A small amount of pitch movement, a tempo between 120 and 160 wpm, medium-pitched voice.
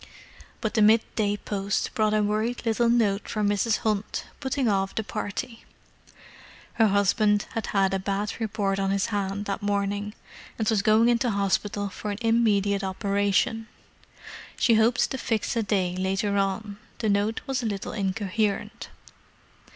No: narrow, 1.9 semitones; average, 155 wpm; high, 210 Hz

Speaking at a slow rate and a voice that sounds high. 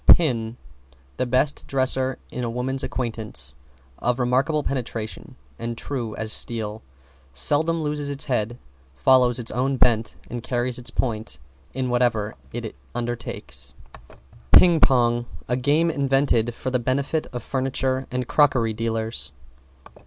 No: slow, 130 wpm; low, 125 Hz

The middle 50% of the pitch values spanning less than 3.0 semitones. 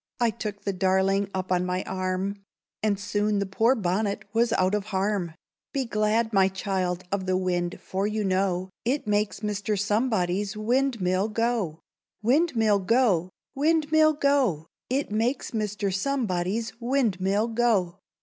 No: average, 3.5 semitones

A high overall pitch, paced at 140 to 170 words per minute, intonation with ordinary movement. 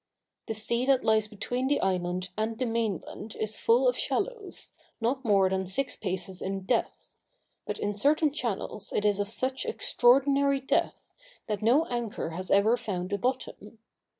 Yes: high, 225 Hz; average, 165 wpm; average, 4.5 semitones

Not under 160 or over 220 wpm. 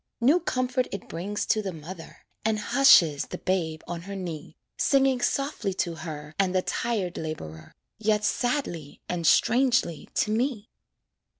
No: average, 145 wpm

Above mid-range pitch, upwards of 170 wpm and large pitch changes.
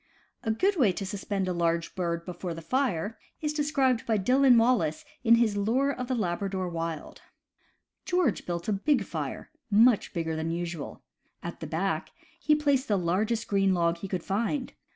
Yes: high, 205 Hz; average, 185 wpm; wide, 6.6 semitones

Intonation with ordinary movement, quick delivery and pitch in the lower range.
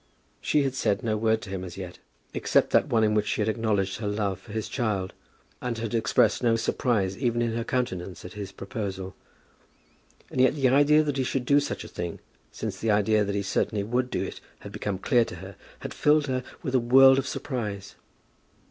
Yes: average, 4.1 semitones; fast, 215 wpm; low, 110 Hz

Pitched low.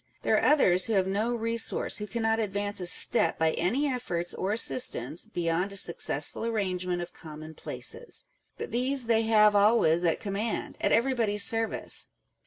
No: high, 205 Hz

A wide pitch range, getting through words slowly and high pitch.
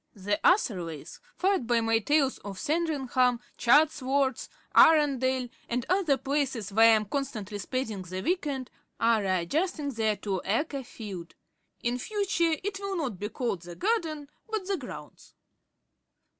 No: wide, 6.3 semitones; average, 145 wpm; very high, 260 Hz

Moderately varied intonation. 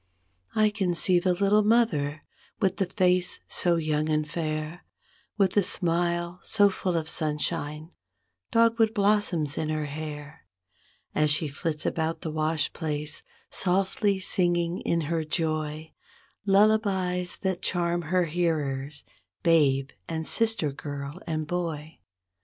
Yes: average, 3.4 semitones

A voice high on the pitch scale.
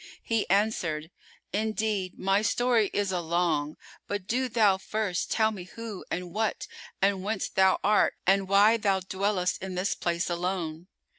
Yes: high, 195 Hz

